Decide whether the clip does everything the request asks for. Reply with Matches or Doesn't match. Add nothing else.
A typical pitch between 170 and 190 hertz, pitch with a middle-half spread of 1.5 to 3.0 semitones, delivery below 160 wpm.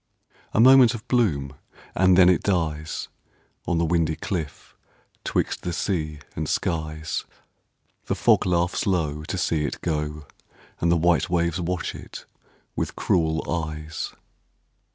Doesn't match